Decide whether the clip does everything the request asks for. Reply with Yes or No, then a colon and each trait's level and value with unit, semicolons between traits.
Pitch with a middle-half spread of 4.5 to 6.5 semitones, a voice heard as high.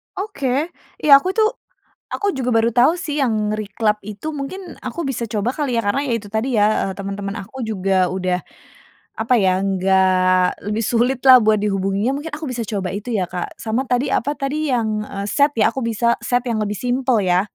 Yes: average, 5.0 semitones; high, 225 Hz